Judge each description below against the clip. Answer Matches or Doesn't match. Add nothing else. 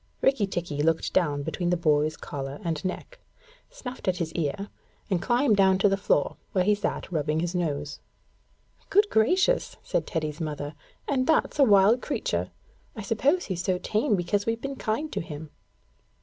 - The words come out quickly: Doesn't match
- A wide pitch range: Matches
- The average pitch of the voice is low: Doesn't match